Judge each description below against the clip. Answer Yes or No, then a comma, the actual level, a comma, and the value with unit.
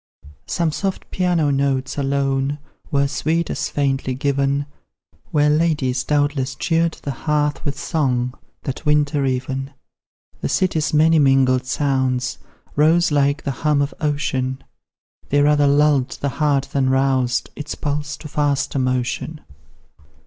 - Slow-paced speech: Yes, slow, 130 wpm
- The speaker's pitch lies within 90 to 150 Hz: Yes, medium, 140 Hz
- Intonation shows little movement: Yes, narrow, 1.9 semitones